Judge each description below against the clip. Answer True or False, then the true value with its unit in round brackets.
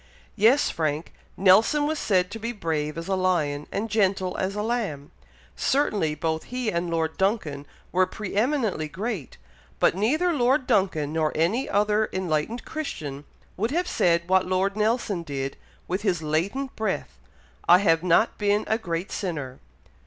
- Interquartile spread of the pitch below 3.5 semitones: False (5.3 semitones)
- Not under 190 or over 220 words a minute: False (160 wpm)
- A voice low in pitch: False (190 Hz)